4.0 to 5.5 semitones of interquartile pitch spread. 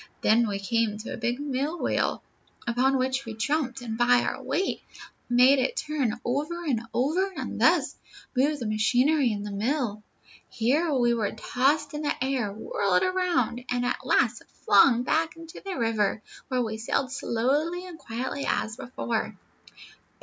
Yes: average, 4.5 semitones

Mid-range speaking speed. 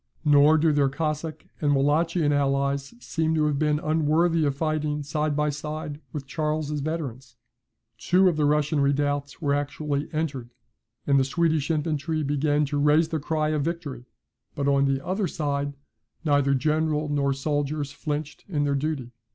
Yes: average, 160 wpm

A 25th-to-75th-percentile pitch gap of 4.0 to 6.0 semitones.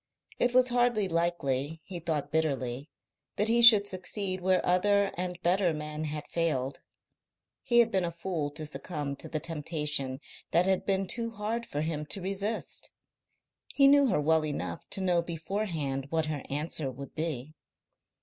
Yes: average, 4.8 semitones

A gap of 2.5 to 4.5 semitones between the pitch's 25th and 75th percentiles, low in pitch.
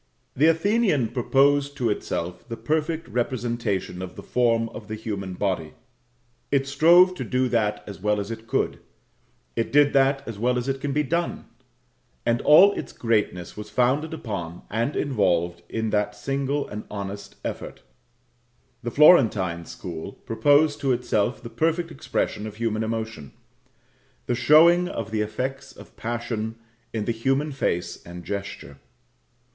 No: average, 5.2 semitones; low, 115 Hz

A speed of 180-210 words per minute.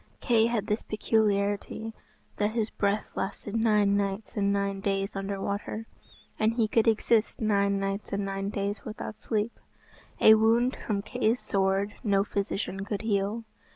No: average, 155 wpm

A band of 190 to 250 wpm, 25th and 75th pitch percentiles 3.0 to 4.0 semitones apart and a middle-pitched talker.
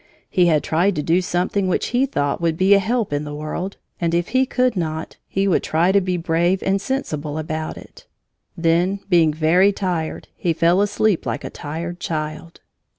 Yes: average, 195 wpm; average, 3.5 semitones; medium, 175 Hz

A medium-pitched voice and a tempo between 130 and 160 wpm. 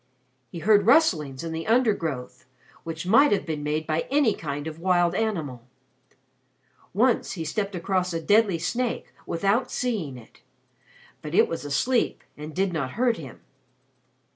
Yes: medium, 175 Hz; average, 150 wpm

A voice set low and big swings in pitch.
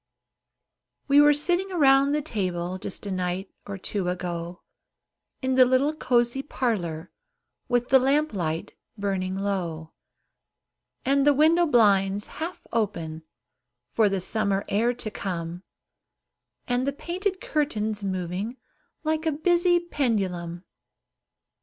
No: high, 220 Hz; wide, 7.5 semitones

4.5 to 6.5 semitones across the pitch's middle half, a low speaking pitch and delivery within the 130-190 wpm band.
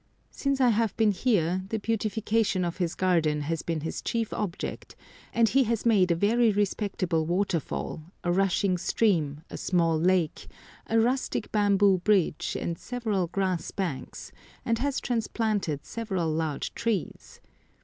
No: average, 4.8 semitones; high, 195 Hz; average, 145 wpm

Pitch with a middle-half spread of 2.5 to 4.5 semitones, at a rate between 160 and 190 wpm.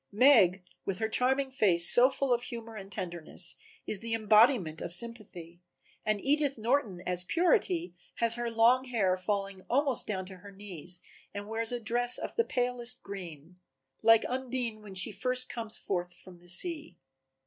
No: average, 5.0 semitones; average, 170 wpm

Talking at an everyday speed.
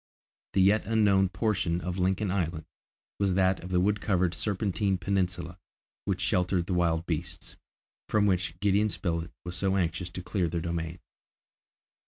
Yes: average, 155 wpm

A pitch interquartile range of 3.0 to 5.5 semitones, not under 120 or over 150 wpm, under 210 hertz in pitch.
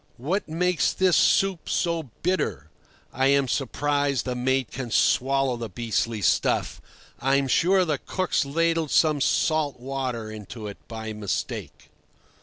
Yes: average, 5.2 semitones; slow, 135 wpm; low, 135 Hz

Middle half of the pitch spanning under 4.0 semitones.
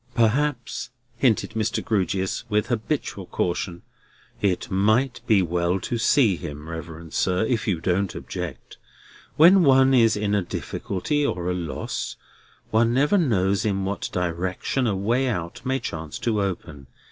No: average, 5.0 semitones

